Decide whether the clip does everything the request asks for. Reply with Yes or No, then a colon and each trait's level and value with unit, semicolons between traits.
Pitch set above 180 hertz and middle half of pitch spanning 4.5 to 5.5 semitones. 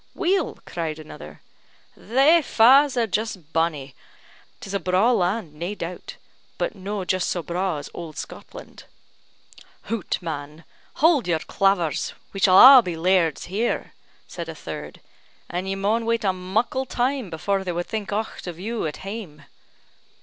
Yes: high, 190 Hz; average, 5.1 semitones